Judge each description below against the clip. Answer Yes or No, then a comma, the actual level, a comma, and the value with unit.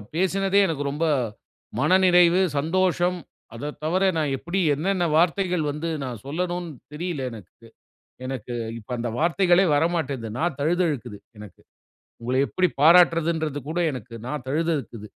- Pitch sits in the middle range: Yes, medium, 165 Hz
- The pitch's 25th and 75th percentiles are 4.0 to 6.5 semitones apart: Yes, average, 4.5 semitones